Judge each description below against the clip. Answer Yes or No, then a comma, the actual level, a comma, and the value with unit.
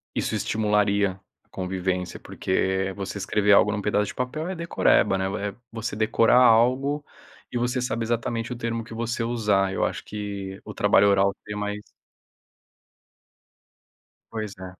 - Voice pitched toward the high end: No, low, 105 Hz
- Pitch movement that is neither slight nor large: Yes, average, 3.0 semitones